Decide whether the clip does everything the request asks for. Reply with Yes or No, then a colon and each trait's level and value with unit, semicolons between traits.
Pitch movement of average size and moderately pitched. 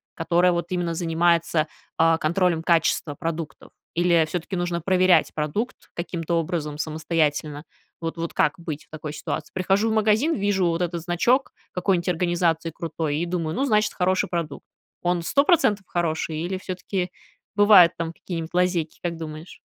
No: narrow, 2.1 semitones; medium, 170 Hz